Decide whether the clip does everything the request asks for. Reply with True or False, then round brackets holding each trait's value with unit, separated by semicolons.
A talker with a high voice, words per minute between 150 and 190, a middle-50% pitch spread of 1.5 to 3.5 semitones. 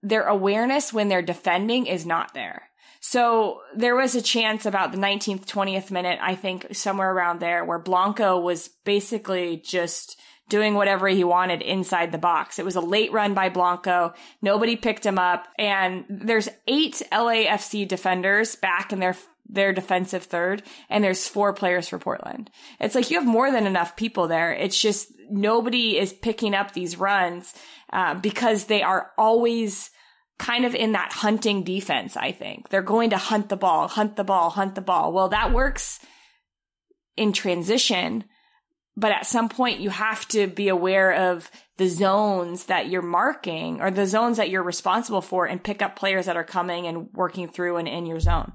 True (195 Hz; 180 wpm; 3.2 semitones)